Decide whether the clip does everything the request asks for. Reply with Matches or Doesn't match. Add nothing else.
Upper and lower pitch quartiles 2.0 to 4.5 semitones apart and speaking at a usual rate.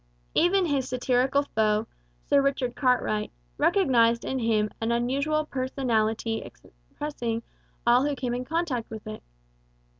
Doesn't match